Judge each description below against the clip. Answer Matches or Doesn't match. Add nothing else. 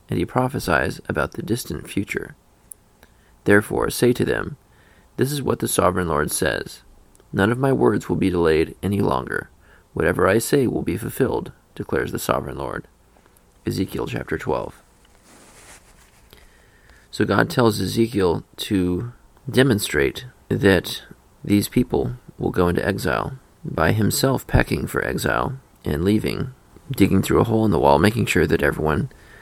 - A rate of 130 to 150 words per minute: Matches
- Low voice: Matches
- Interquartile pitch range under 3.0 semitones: Doesn't match